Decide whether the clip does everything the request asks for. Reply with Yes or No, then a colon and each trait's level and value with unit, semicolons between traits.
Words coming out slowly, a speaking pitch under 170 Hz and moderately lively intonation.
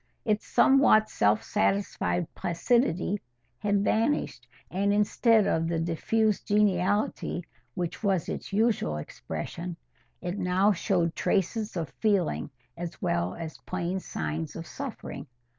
No: slow, 120 wpm; medium, 185 Hz; average, 4.2 semitones